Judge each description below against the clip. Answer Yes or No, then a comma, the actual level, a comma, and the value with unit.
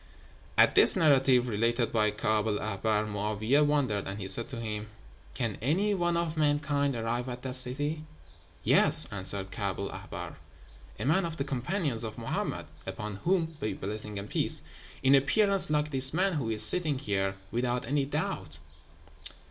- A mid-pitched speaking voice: No, low, 125 Hz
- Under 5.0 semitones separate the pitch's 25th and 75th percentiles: No, wide, 5.6 semitones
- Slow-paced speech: No, average, 165 wpm